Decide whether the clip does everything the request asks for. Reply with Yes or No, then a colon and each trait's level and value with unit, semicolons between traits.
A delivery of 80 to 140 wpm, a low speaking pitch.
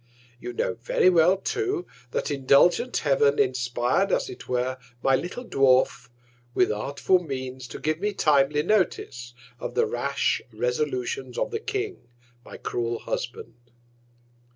No: slow, 135 wpm; medium, 150 Hz